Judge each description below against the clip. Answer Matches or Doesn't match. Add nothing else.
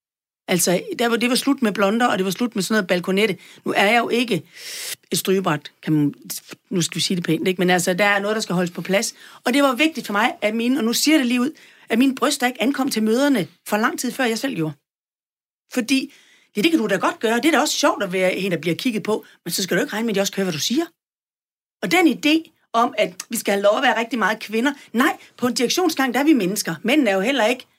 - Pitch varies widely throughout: Matches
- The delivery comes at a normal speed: Doesn't match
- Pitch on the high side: Matches